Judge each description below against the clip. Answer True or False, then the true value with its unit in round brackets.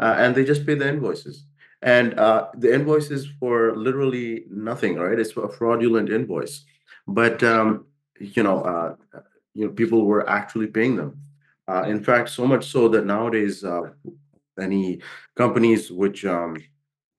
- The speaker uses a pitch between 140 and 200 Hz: False (115 Hz)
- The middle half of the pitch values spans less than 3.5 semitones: False (4.6 semitones)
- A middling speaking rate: True (155 wpm)